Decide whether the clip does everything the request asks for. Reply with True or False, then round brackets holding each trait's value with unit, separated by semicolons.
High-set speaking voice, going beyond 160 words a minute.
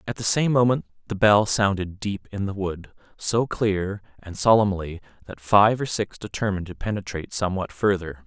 False (100 Hz; 175 wpm)